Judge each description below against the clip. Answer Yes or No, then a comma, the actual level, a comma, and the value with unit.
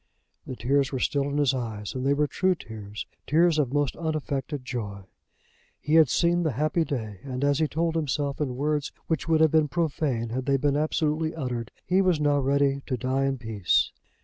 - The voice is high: No, medium, 140 Hz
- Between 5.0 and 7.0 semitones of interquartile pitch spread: No, average, 3.4 semitones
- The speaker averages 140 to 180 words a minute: No, average, 200 wpm